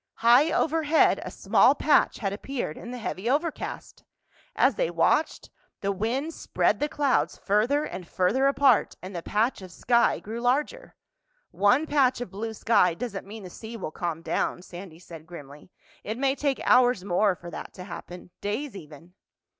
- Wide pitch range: Yes, wide, 6.6 semitones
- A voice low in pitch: No, high, 220 Hz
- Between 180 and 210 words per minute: No, average, 170 wpm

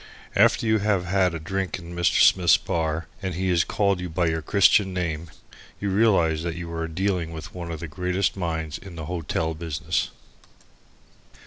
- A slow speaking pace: No, average, 185 wpm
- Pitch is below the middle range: Yes, very low, 85 Hz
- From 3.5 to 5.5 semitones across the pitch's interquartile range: No, narrow, 2.6 semitones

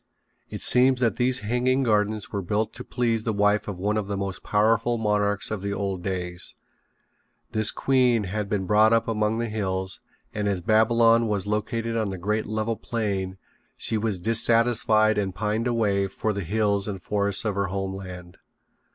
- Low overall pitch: Yes, low, 105 Hz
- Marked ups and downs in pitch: No, narrow, 2.4 semitones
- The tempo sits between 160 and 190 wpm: Yes, average, 180 wpm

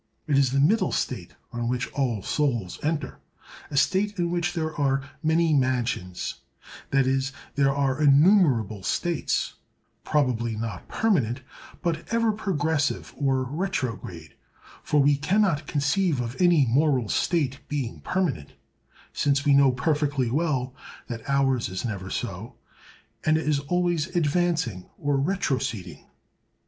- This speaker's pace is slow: Yes, slow, 130 wpm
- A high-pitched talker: No, medium, 140 Hz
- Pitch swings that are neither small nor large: Yes, average, 4.2 semitones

